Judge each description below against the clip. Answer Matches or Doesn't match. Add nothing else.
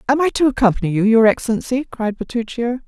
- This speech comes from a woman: Matches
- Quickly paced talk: Doesn't match